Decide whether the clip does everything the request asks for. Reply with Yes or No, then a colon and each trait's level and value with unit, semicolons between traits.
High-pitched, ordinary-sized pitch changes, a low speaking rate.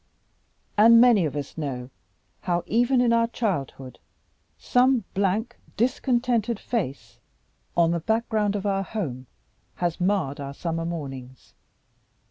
No: high, 195 Hz; wide, 7.6 semitones; slow, 120 wpm